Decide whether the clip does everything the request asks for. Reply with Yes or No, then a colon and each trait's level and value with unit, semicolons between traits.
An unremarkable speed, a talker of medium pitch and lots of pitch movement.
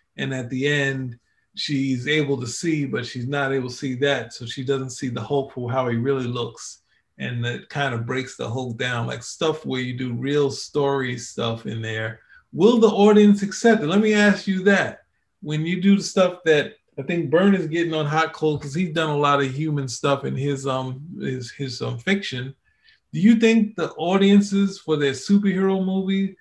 No: fast, 210 wpm; medium, 145 Hz; wide, 6.3 semitones